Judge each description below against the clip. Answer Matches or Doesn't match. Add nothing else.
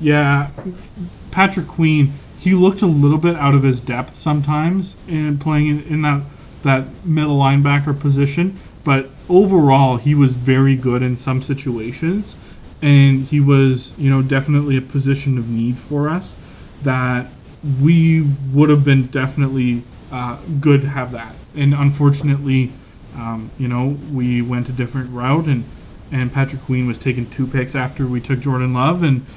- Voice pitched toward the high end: Doesn't match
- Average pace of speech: Matches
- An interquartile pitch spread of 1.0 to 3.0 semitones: Matches